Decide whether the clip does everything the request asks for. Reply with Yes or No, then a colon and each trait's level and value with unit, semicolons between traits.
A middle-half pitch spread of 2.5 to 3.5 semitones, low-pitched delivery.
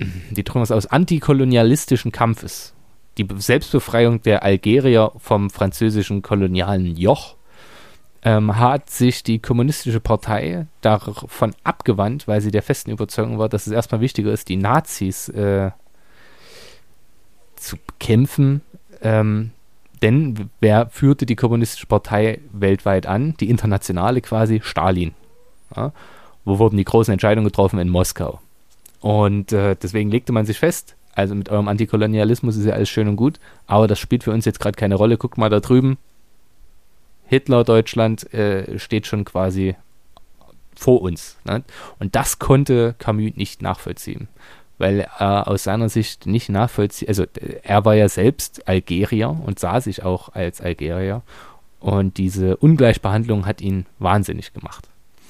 Yes: average, 3.0 semitones; low, 110 Hz